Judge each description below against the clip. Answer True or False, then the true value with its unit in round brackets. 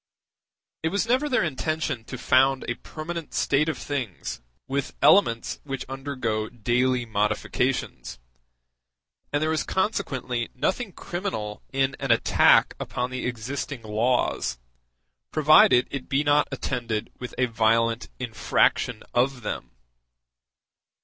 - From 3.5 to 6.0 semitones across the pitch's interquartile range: True (4.0 semitones)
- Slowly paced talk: True (120 wpm)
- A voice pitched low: True (130 Hz)